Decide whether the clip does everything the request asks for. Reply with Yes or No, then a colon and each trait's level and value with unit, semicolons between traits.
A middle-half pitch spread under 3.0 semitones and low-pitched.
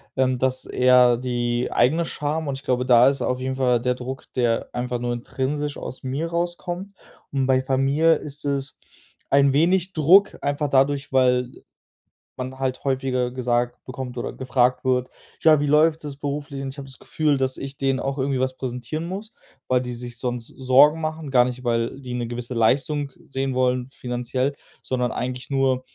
Yes: narrow, 2.4 semitones; low, 130 Hz